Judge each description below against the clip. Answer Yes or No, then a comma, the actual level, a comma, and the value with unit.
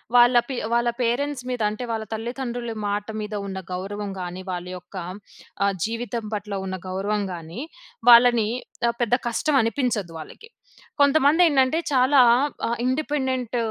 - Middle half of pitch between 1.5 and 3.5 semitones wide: No, average, 3.9 semitones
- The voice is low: No, high, 235 Hz